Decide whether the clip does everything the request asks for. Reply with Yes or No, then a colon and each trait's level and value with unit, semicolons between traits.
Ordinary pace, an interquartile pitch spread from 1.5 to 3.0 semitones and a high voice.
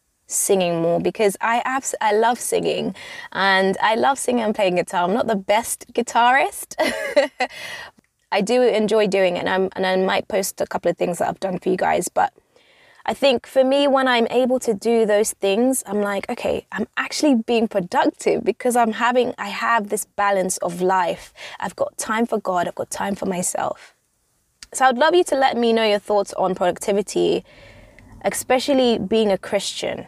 No: average, 190 wpm; average, 4.8 semitones; high, 225 Hz